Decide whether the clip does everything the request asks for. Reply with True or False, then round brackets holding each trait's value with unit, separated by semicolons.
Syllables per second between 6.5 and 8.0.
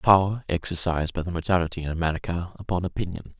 True (6.7 syllables/s)